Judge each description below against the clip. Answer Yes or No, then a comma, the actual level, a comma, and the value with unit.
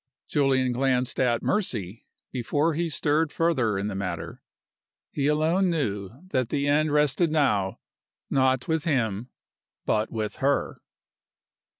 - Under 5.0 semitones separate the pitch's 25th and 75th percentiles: No, average, 5.3 semitones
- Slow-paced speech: Yes, slow, 125 wpm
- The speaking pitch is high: No, low, 135 Hz